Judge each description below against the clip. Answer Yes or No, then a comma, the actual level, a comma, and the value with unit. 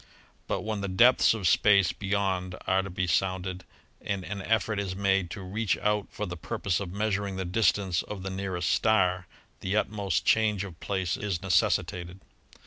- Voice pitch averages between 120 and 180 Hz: No, very low, 95 Hz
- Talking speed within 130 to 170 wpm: No, average, 180 wpm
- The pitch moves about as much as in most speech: No, narrow, 2.0 semitones